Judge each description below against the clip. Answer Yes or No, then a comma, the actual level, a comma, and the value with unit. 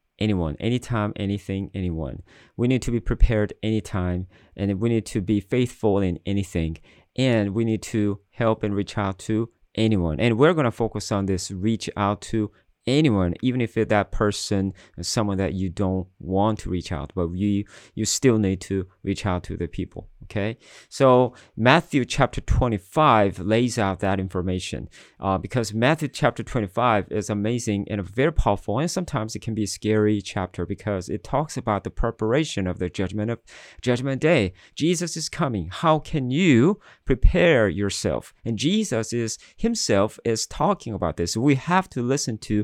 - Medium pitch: No, low, 105 Hz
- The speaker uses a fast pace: No, average, 175 wpm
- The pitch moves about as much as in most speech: Yes, average, 3.6 semitones